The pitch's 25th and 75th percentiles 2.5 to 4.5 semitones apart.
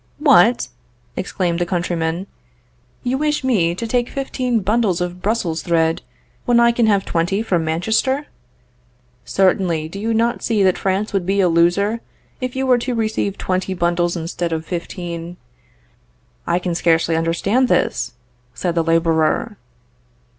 No: average, 5.0 semitones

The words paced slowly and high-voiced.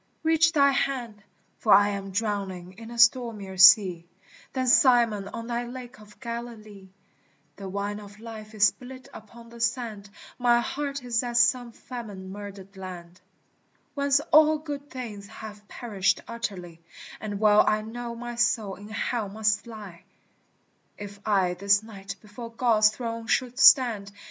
No: average, 150 wpm; high, 220 Hz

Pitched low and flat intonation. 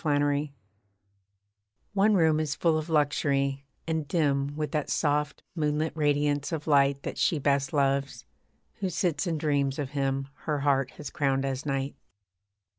No: medium, 145 Hz; narrow, 2.0 semitones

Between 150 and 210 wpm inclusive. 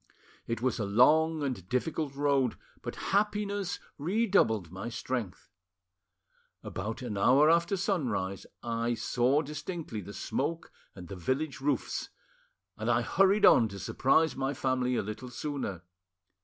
No: slow, 135 wpm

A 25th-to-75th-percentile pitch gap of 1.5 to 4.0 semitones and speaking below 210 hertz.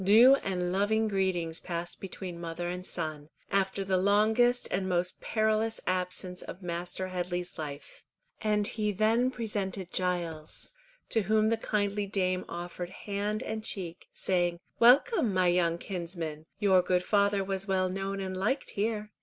Yes: average, 3.0 semitones; high, 190 Hz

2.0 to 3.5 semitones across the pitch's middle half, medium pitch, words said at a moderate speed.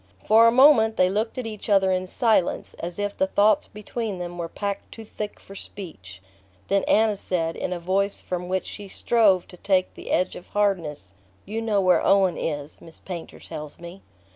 No: average, 3.2 semitones; high, 195 Hz; average, 195 wpm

